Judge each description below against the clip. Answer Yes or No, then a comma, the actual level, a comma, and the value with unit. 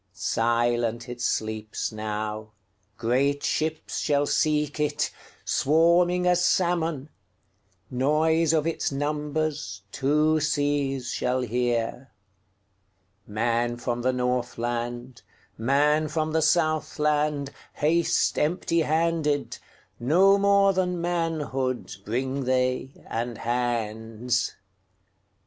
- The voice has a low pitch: Yes, low, 130 Hz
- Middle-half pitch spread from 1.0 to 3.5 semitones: No, average, 5.0 semitones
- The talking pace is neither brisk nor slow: No, slow, 70 wpm